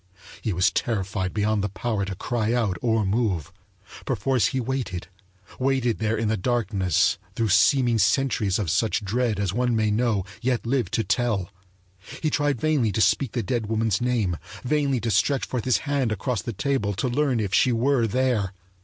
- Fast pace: No, average, 180 wpm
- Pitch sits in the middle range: No, low, 115 Hz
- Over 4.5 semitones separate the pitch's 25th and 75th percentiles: No, average, 3.7 semitones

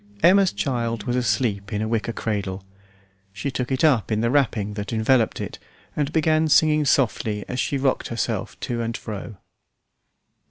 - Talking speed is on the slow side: No, average, 165 wpm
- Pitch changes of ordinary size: Yes, average, 4.4 semitones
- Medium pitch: No, low, 115 Hz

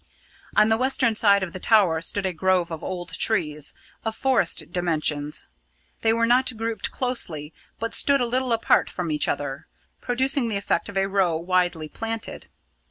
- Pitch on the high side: Yes, high, 195 Hz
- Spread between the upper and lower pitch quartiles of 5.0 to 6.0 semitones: Yes, wide, 5.4 semitones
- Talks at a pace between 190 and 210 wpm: No, average, 170 wpm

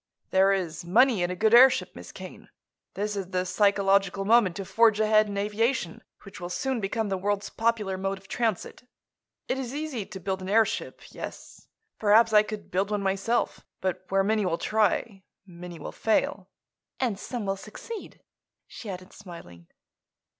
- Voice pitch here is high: Yes, high, 200 Hz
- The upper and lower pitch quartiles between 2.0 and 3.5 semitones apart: Yes, narrow, 2.6 semitones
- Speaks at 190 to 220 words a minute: No, average, 170 wpm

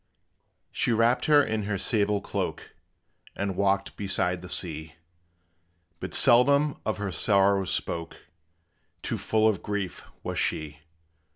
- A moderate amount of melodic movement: Yes, average, 3.1 semitones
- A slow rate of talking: Yes, slow, 125 wpm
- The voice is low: Yes, low, 100 Hz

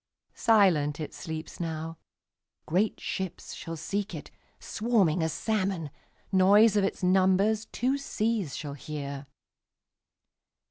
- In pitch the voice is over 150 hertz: Yes, medium, 185 Hz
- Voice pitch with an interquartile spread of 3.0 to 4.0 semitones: No, average, 4.9 semitones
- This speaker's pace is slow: Yes, slow, 90 wpm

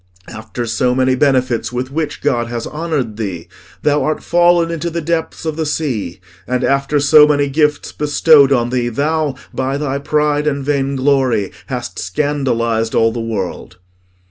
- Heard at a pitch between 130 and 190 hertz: Yes, medium, 140 Hz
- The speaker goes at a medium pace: Yes, average, 160 wpm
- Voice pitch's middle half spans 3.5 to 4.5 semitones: Yes, average, 3.9 semitones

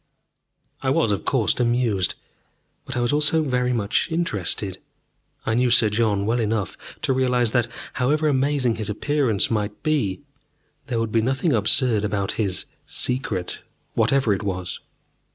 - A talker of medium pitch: No, low, 120 Hz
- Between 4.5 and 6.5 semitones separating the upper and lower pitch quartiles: No, average, 3.9 semitones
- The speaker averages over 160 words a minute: No, average, 150 wpm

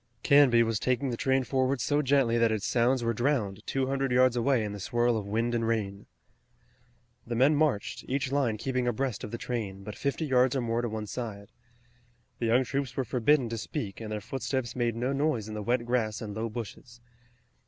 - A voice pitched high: No, low, 120 Hz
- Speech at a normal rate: No, fast, 210 wpm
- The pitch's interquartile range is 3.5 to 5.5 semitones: No, average, 3.1 semitones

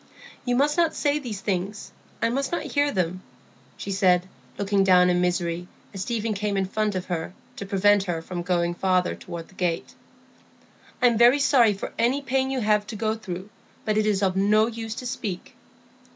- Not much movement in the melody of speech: No, average, 4.0 semitones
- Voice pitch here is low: No, high, 205 Hz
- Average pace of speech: Yes, average, 195 wpm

